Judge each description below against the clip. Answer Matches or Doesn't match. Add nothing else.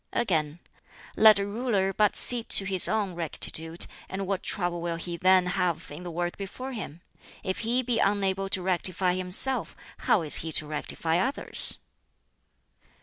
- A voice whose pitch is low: Doesn't match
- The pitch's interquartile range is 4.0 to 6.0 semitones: Doesn't match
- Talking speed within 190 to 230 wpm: Doesn't match